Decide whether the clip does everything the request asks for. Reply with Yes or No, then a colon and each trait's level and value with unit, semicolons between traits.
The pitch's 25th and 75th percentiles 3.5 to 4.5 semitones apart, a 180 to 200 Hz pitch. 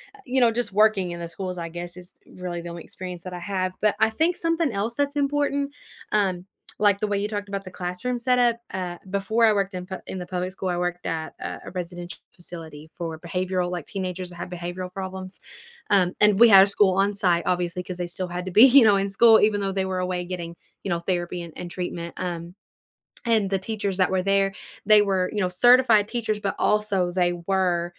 No: average, 2.8 semitones; medium, 185 Hz